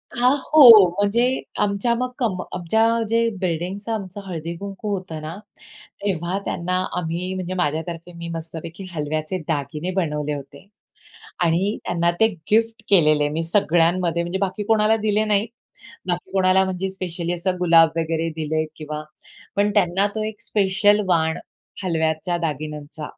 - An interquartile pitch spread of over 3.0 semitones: Yes, average, 3.7 semitones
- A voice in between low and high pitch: Yes, medium, 180 Hz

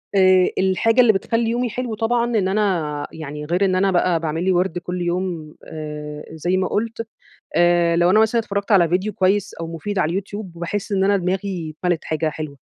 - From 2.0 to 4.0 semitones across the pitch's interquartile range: Yes, average, 3.4 semitones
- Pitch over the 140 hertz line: Yes, medium, 185 Hz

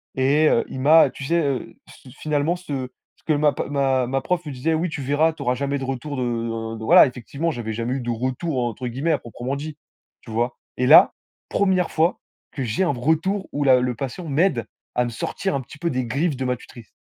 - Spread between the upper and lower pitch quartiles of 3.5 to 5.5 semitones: Yes, average, 4.1 semitones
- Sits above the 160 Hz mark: No, low, 135 Hz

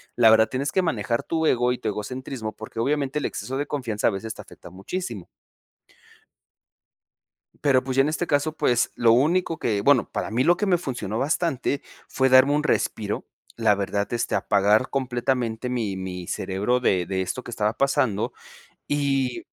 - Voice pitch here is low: Yes, low, 125 Hz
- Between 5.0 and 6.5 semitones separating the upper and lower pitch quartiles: No, average, 4.5 semitones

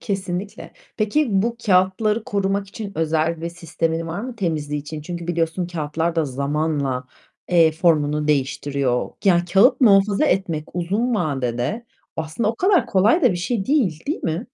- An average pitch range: Yes, average, 4.7 semitones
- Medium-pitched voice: Yes, medium, 175 Hz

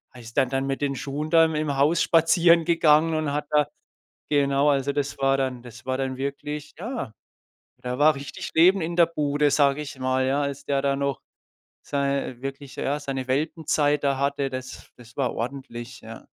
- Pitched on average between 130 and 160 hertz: Yes, medium, 140 Hz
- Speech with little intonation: Yes, narrow, 2.0 semitones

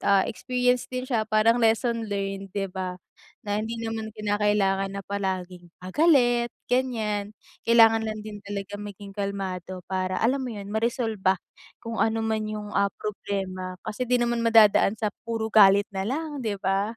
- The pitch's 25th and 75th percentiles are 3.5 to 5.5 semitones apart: No, narrow, 2.6 semitones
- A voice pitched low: No, high, 215 Hz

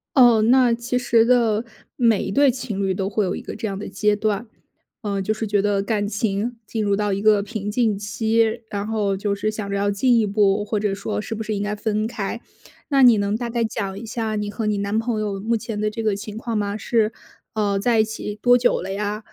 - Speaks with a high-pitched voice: Yes, high, 215 Hz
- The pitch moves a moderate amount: No, narrow, 1.9 semitones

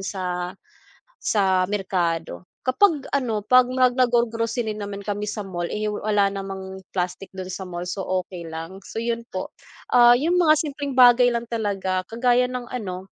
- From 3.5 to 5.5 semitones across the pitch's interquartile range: Yes, average, 4.5 semitones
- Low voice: No, high, 210 Hz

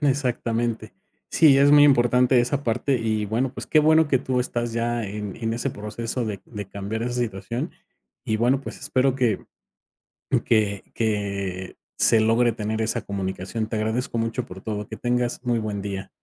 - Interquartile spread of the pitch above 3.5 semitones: No, average, 2.8 semitones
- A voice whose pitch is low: Yes, low, 115 Hz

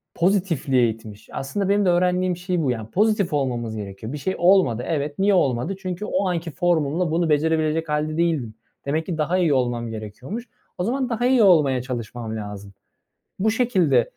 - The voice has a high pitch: No, medium, 155 Hz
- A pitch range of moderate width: No, wide, 6.9 semitones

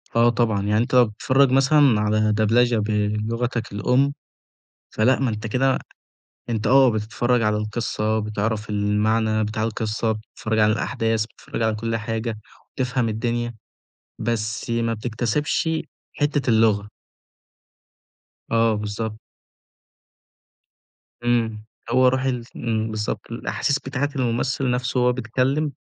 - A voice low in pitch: Yes, low, 115 Hz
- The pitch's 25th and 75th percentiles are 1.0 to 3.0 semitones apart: Yes, narrow, 2.4 semitones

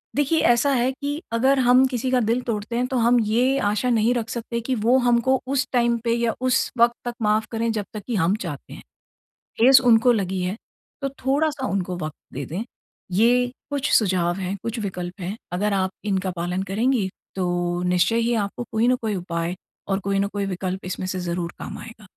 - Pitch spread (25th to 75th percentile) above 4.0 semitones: Yes, average, 4.7 semitones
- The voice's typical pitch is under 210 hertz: No, high, 225 Hz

